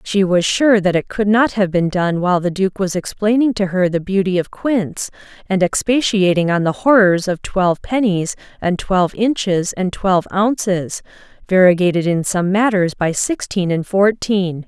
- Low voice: No, high, 190 Hz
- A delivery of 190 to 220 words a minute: No, average, 170 wpm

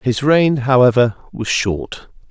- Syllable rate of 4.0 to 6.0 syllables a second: No, 3.5 syllables/s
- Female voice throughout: No, male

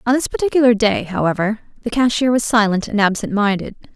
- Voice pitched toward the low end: No, high, 220 Hz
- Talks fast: No, average, 180 wpm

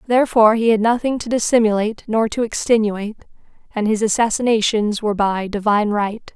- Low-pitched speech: No, high, 220 Hz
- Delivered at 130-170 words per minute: Yes, average, 150 wpm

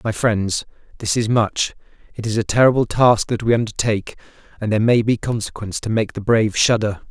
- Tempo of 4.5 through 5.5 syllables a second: No, 5.9 syllables/s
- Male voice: Yes, male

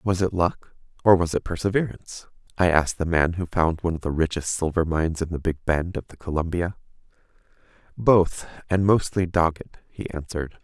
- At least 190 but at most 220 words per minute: No, average, 180 wpm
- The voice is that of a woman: No, male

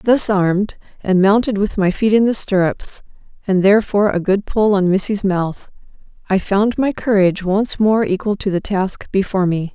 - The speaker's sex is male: No, female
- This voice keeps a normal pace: Yes, average, 185 wpm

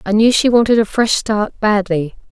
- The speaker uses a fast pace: Yes, fast, 210 wpm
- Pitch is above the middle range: Yes, high, 215 Hz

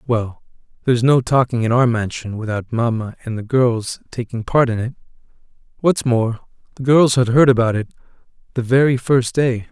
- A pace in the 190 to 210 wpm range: No, average, 175 wpm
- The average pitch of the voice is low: Yes, low, 120 Hz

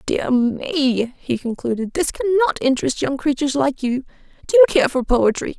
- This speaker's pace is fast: No, average, 170 wpm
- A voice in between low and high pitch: No, very high, 275 Hz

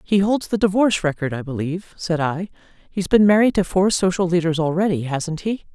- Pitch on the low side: No, medium, 180 Hz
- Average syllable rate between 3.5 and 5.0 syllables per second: No, 5.6 syllables/s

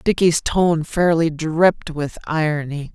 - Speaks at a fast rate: No, slow, 120 wpm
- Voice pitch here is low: No, medium, 160 Hz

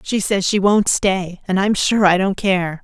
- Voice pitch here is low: No, high, 190 Hz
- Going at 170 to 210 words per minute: No, fast, 235 wpm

